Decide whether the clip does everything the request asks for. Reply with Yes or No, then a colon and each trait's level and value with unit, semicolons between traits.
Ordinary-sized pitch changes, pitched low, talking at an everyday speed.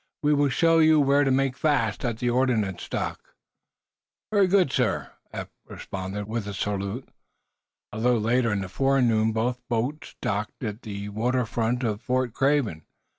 Yes: average, 4.2 semitones; low, 120 Hz; average, 165 wpm